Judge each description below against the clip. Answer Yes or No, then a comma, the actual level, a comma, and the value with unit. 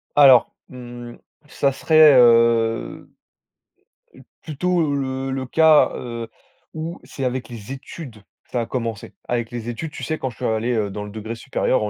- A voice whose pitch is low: Yes, low, 125 Hz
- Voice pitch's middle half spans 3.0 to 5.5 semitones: Yes, average, 3.3 semitones